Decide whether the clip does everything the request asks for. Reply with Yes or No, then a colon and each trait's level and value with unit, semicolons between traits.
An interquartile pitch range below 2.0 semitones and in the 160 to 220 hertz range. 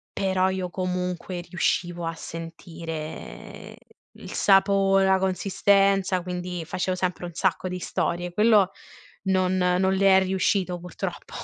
Yes: narrow, 1.4 semitones; medium, 185 Hz